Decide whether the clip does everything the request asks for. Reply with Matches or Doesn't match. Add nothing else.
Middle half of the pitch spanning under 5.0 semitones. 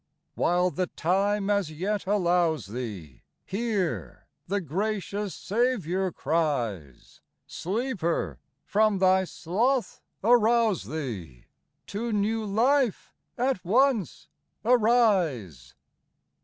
Doesn't match